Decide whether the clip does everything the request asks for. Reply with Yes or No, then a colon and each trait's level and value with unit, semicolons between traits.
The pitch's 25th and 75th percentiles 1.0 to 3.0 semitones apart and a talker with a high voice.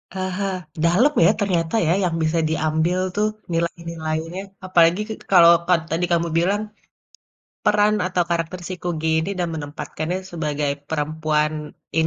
No: narrow, 2.4 semitones; medium, 170 Hz